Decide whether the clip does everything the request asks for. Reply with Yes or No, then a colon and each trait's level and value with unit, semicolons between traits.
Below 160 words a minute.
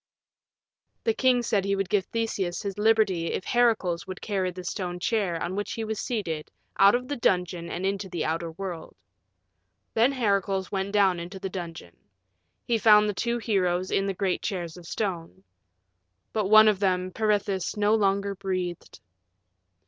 No: average, 170 wpm